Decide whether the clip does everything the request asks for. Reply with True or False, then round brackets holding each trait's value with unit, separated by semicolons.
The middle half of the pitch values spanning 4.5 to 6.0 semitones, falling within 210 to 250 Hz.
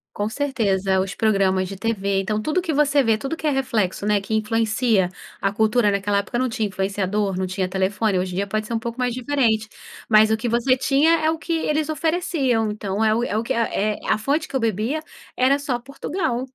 True (4.9 semitones; 220 Hz)